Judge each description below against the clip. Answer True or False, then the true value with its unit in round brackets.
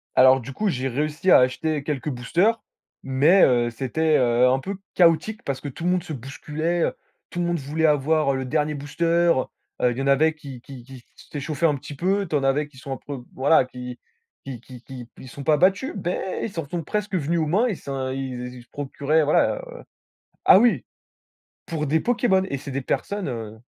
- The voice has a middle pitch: True (145 Hz)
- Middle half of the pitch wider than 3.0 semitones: True (4.3 semitones)